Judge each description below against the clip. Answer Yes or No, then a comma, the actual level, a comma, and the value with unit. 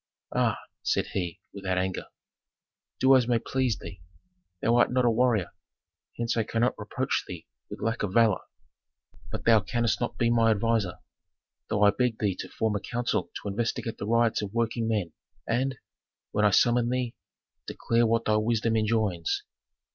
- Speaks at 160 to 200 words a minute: Yes, average, 170 wpm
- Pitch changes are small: Yes, narrow, 2.3 semitones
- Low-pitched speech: Yes, low, 115 Hz